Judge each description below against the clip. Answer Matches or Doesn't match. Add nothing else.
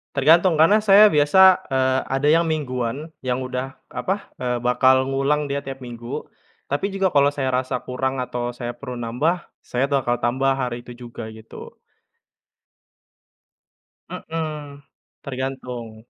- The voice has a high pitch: Doesn't match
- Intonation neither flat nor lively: Matches